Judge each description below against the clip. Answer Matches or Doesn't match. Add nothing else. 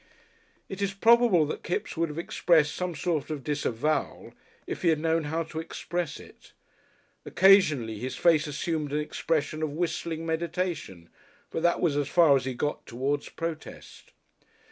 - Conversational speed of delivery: Matches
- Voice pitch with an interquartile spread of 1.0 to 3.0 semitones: Matches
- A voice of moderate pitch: Matches